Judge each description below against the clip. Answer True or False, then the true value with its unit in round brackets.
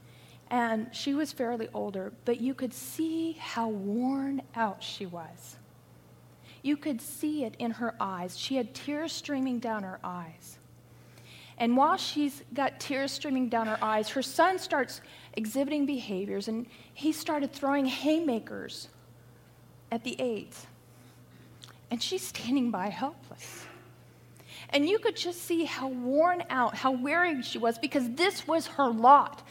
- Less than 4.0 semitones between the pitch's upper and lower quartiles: False (4.9 semitones)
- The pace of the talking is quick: False (145 wpm)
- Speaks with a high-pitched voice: True (255 Hz)